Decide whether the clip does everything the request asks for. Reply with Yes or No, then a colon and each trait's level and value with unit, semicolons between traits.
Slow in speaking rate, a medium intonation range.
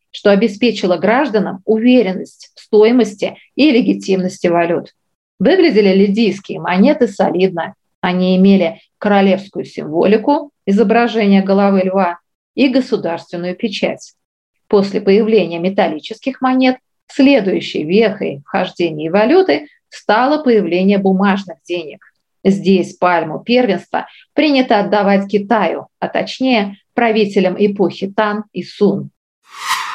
Yes: slow, 95 wpm; average, 3.7 semitones